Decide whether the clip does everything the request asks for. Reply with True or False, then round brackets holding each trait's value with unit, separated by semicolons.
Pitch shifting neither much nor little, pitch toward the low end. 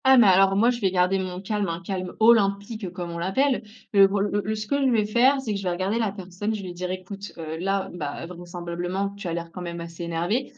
False (3.1 semitones; 195 Hz)